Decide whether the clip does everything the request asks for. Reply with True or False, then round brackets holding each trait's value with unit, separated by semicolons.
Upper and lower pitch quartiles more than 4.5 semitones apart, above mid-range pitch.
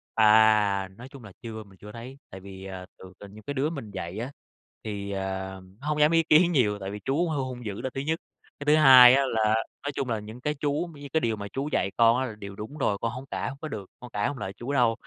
False (5.4 semitones; 115 Hz)